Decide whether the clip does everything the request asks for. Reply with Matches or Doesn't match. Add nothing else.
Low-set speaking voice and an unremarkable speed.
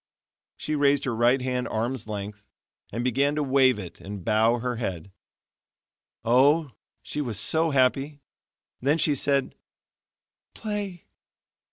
Doesn't match